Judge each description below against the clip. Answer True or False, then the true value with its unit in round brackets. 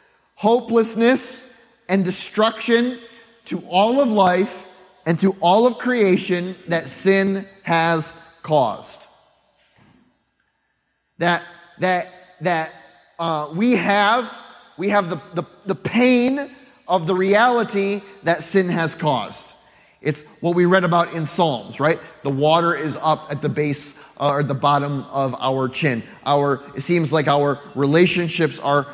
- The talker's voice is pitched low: False (175 Hz)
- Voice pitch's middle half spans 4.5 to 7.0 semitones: True (4.8 semitones)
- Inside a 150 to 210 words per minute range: False (135 wpm)